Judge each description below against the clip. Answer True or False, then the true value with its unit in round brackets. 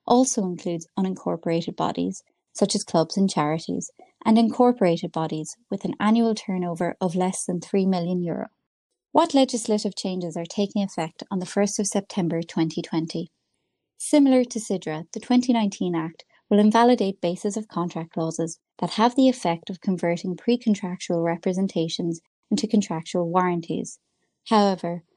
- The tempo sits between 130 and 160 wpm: True (140 wpm)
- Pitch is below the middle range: False (190 Hz)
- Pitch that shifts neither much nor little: True (4.3 semitones)